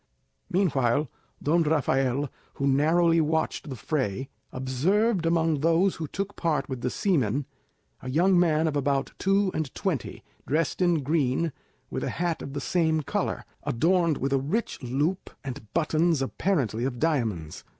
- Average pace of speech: Yes, average, 150 wpm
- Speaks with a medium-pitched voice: Yes, medium, 155 Hz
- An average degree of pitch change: Yes, average, 4.0 semitones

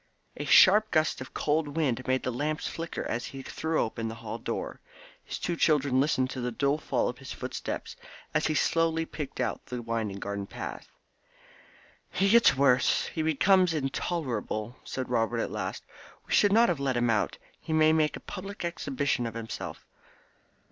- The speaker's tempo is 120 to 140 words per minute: No, average, 180 wpm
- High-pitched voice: No, medium, 140 Hz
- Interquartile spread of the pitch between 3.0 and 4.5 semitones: No, average, 4.9 semitones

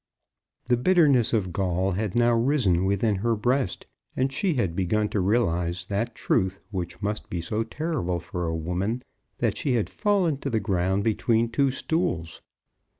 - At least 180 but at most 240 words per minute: No, average, 165 wpm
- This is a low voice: Yes, low, 105 Hz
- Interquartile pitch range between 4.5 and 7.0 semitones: Yes, average, 5.2 semitones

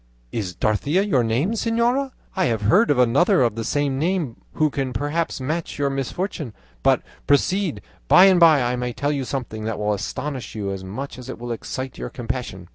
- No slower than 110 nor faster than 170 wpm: No, average, 200 wpm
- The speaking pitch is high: No, low, 135 Hz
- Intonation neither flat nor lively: No, wide, 6.2 semitones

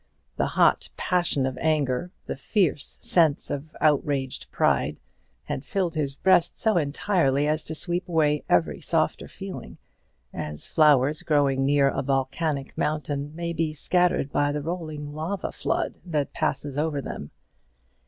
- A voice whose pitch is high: No, medium, 150 Hz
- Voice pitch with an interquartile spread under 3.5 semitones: Yes, average, 2.9 semitones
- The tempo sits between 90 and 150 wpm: Yes, average, 145 wpm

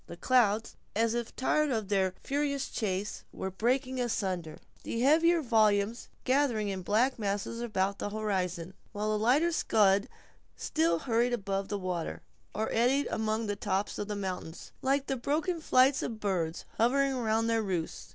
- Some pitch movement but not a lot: Yes, average, 4.4 semitones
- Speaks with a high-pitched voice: Yes, high, 220 Hz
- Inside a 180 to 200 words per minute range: No, average, 160 wpm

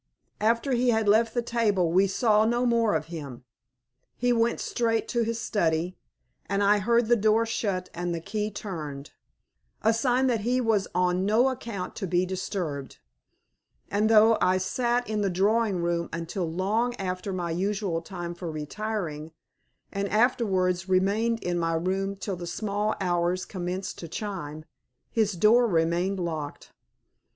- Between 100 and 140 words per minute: No, average, 160 wpm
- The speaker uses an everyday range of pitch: Yes, average, 4.3 semitones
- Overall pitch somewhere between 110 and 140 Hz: No, high, 195 Hz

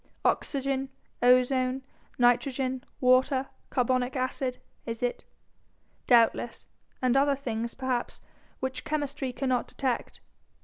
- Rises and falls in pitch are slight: Yes, narrow, 1.4 semitones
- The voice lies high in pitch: Yes, very high, 255 Hz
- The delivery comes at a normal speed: No, slow, 95 wpm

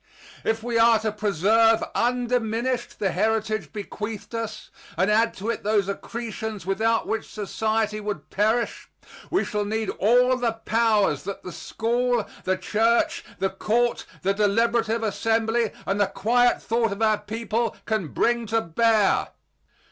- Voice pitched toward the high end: Yes, high, 220 Hz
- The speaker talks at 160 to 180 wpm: No, average, 145 wpm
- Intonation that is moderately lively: No, narrow, 1.8 semitones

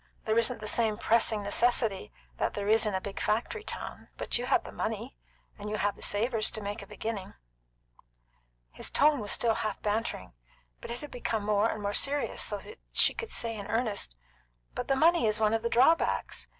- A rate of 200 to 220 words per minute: Yes, fast, 205 wpm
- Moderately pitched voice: No, high, 220 Hz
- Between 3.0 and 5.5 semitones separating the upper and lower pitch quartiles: No, narrow, 2.6 semitones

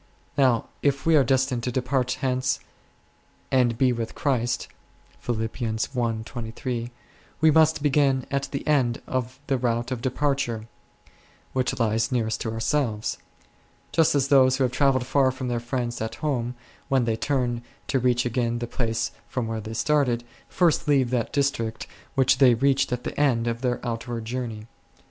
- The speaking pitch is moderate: No, low, 125 Hz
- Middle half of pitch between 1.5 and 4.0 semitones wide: Yes, narrow, 2.6 semitones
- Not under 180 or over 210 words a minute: No, average, 160 wpm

